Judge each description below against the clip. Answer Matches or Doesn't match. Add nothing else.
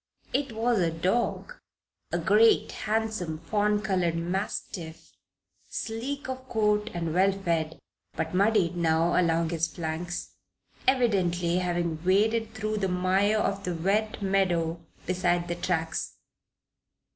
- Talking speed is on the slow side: Matches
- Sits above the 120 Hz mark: Matches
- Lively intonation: Doesn't match